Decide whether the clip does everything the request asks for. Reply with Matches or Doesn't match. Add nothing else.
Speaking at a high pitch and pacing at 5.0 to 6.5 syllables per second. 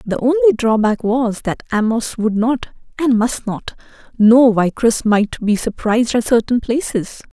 Doesn't match